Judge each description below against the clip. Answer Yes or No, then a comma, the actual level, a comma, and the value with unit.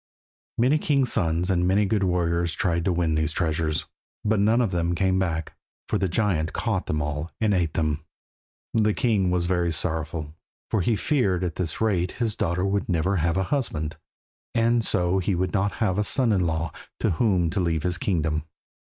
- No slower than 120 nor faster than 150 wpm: No, average, 195 wpm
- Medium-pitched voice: No, very low, 90 Hz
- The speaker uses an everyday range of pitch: Yes, average, 3.8 semitones